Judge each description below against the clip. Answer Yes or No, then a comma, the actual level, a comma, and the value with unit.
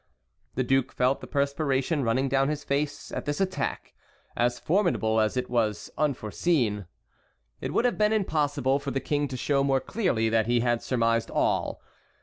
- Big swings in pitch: No, average, 3.6 semitones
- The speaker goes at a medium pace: Yes, average, 170 wpm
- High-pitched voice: No, low, 135 Hz